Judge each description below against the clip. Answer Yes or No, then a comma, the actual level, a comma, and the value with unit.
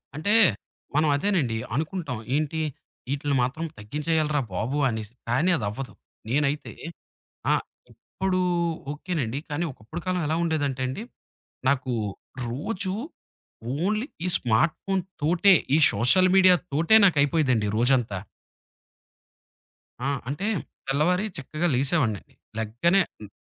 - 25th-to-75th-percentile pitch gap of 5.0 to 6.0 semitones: Yes, wide, 5.6 semitones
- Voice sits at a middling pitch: Yes, medium, 150 Hz